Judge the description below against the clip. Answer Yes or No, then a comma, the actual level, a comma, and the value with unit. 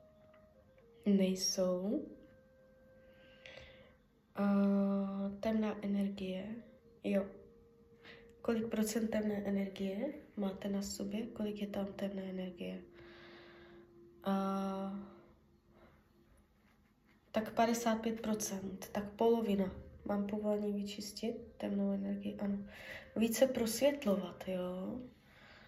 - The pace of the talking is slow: Yes, slow, 70 wpm